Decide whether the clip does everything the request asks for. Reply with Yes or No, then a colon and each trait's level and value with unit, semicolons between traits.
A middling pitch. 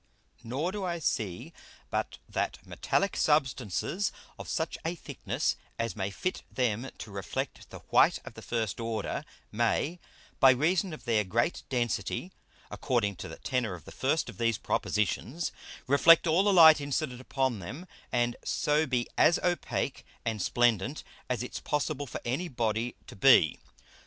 No: low, 125 Hz